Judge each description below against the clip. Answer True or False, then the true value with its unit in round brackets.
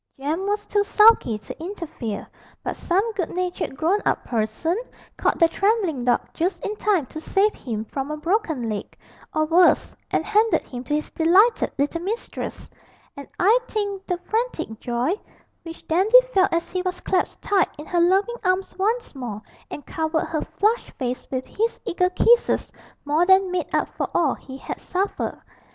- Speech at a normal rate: True (175 wpm)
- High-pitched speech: True (355 Hz)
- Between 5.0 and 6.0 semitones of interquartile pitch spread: True (5.5 semitones)